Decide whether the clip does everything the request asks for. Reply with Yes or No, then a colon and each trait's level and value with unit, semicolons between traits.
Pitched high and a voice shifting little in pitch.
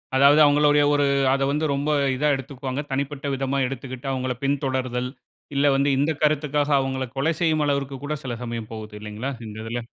No: low, 135 Hz; narrow, 2.1 semitones